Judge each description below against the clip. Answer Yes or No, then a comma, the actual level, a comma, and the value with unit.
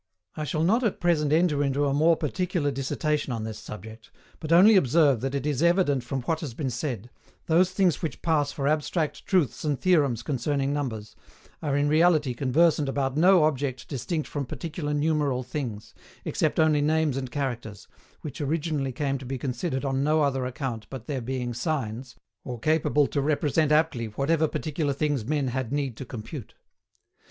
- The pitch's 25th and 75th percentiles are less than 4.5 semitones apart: Yes, average, 3.2 semitones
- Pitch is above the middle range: No, medium, 145 Hz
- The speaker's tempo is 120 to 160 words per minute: No, average, 180 wpm